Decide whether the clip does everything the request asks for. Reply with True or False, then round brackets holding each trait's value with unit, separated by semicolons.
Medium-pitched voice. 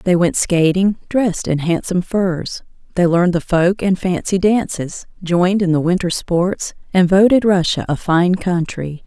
True (180 Hz)